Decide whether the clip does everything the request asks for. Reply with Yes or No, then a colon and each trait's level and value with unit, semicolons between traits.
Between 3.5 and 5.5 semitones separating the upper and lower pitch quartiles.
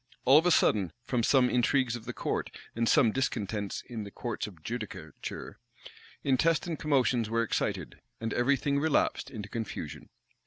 Yes: average, 3.8 semitones